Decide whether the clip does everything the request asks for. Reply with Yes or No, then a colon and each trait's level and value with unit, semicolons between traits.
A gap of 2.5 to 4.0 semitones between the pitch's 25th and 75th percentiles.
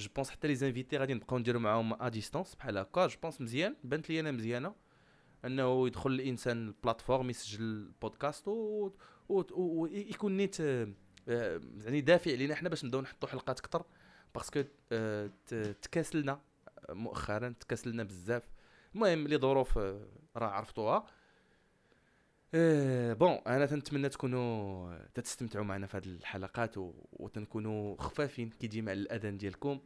No: average, 4.9 semitones